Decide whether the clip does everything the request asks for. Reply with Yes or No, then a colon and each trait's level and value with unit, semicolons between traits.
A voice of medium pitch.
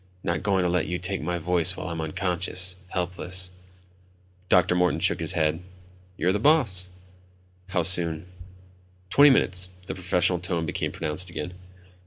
No: very low, 90 Hz